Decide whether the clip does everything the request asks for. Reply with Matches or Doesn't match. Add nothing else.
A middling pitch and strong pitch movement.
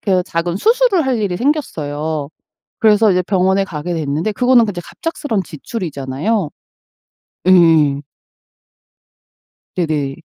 Matches